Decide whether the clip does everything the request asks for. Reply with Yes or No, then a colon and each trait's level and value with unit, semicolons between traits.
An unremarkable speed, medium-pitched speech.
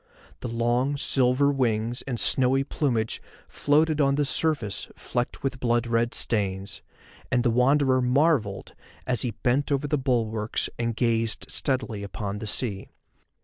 No: average, 145 wpm; low, 125 Hz